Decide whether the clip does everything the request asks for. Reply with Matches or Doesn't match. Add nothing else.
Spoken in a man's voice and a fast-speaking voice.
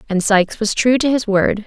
Doesn't match